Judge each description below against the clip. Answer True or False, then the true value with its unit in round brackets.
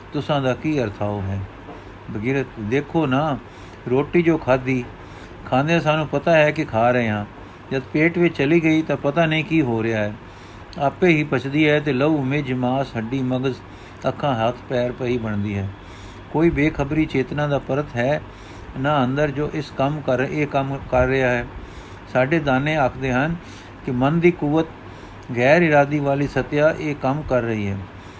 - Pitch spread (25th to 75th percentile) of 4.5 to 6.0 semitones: True (5.1 semitones)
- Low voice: True (130 Hz)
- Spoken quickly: True (170 wpm)